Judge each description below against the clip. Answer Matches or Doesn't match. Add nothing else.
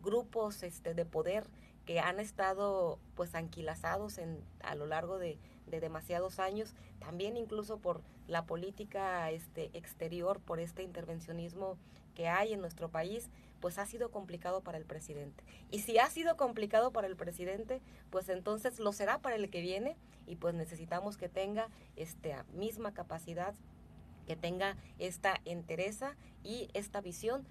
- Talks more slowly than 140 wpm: Doesn't match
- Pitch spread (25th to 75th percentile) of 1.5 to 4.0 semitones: Matches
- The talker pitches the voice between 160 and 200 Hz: Matches